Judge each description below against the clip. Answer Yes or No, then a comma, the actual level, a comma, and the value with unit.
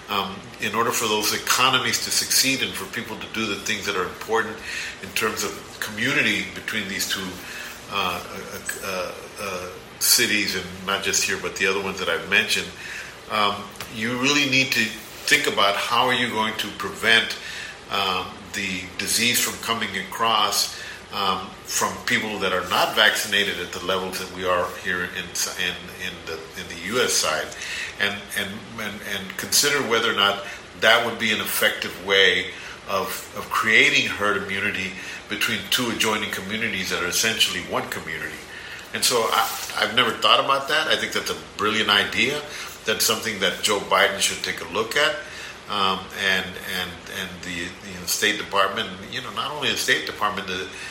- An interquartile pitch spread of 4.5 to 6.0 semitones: No, average, 2.8 semitones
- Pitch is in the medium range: No, low, 100 Hz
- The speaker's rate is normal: Yes, average, 180 wpm